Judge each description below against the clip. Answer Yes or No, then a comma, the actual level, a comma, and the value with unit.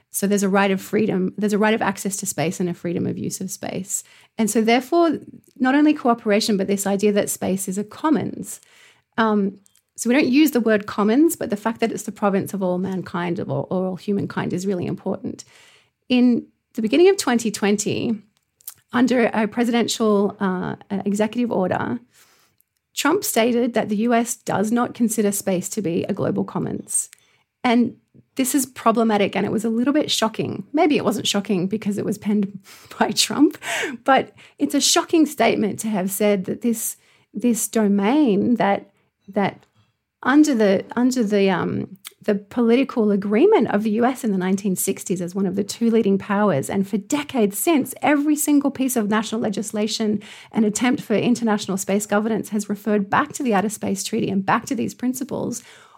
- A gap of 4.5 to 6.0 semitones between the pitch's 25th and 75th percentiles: No, average, 3.4 semitones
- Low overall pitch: No, high, 215 Hz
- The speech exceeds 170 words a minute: Yes, average, 180 wpm